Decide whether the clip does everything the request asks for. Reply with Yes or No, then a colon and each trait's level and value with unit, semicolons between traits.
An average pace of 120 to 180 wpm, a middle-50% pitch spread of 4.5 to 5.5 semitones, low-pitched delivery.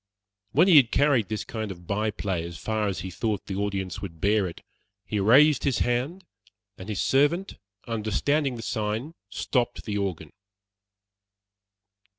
Yes: average, 160 wpm; average, 4.8 semitones; low, 110 Hz